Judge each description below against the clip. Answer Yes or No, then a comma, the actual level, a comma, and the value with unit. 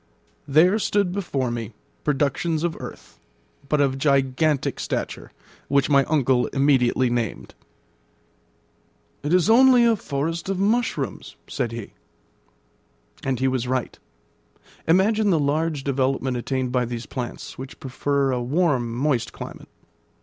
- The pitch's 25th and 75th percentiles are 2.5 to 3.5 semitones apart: No, average, 4.3 semitones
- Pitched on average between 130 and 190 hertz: Yes, medium, 140 Hz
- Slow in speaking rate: Yes, slow, 130 wpm